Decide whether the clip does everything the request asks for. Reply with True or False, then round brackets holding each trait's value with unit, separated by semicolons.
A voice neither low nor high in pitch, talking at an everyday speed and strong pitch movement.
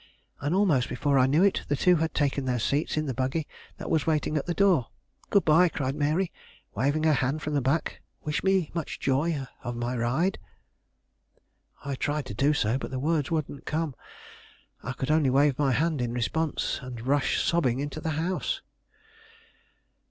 False (145 Hz; 185 wpm; 3.4 semitones)